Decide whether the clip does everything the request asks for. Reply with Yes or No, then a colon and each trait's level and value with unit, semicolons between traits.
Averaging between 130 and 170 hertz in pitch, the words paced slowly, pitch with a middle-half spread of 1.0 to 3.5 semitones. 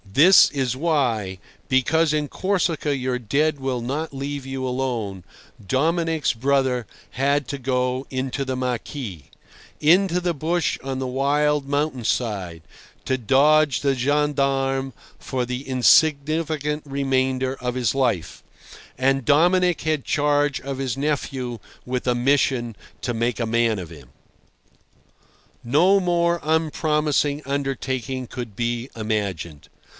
Yes: low, 135 Hz; slow, 120 wpm; average, 3.1 semitones